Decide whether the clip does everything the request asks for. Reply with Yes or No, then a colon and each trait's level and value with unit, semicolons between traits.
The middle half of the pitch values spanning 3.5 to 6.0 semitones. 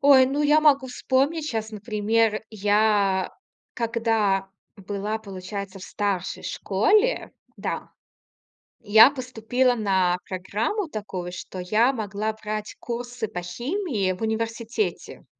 Yes: average, 3.9 semitones